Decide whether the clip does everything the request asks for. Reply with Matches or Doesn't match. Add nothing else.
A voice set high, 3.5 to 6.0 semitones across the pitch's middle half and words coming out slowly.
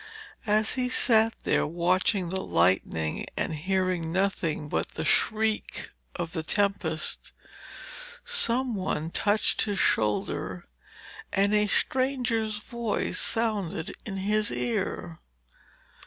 Matches